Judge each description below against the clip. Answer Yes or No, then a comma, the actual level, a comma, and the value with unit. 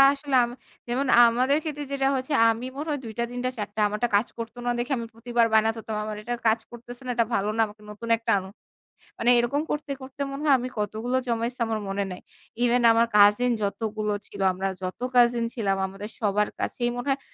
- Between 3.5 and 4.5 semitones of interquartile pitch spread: No, average, 2.9 semitones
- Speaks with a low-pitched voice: No, high, 235 Hz